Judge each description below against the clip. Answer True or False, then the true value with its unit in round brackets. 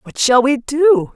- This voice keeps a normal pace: False (210 wpm)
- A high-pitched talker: True (270 Hz)